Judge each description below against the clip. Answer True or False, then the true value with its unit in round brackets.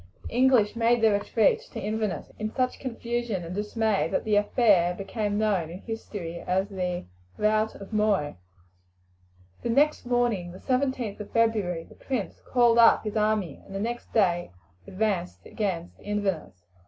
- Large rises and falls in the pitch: False (3.3 semitones)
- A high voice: True (210 Hz)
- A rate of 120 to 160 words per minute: True (155 wpm)